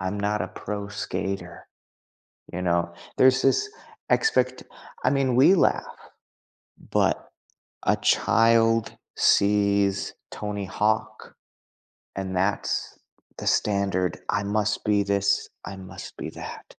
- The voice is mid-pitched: No, low, 100 Hz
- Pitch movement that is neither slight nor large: No, narrow, 2.2 semitones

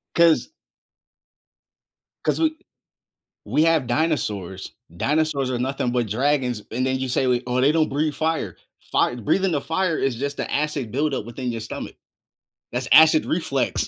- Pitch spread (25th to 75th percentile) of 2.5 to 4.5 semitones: Yes, average, 4.1 semitones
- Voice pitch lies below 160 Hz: Yes, low, 135 Hz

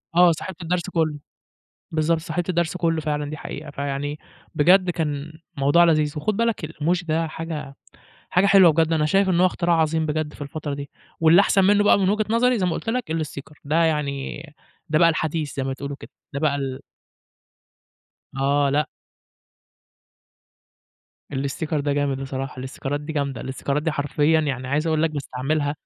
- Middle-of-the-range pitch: Yes, medium, 155 Hz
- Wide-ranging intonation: No, average, 2.9 semitones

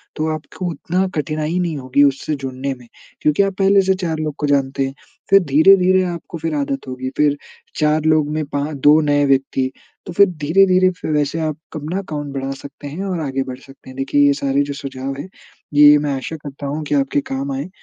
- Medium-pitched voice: Yes, medium, 145 Hz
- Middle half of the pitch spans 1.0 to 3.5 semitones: Yes, average, 2.7 semitones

